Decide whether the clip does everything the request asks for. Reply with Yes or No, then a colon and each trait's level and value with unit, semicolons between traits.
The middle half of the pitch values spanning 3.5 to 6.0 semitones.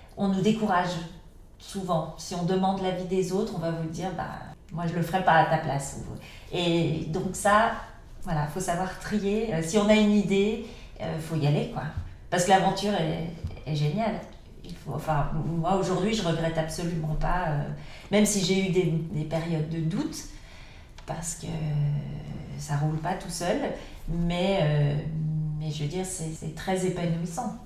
No: average, 3.1 semitones